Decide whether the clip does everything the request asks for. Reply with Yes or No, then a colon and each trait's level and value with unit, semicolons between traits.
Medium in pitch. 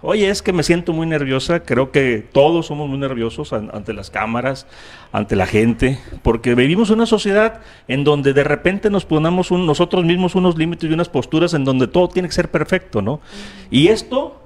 Yes: medium, 150 Hz